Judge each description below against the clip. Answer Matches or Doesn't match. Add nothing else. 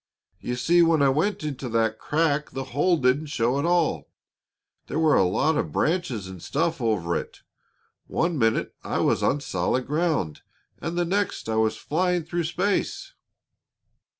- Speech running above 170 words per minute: Doesn't match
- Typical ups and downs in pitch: Doesn't match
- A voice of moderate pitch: Matches